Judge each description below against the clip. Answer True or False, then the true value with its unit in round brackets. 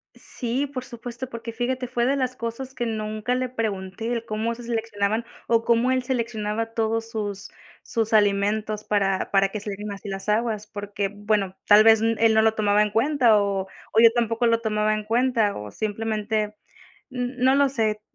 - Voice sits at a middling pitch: False (225 Hz)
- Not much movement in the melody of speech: True (2.2 semitones)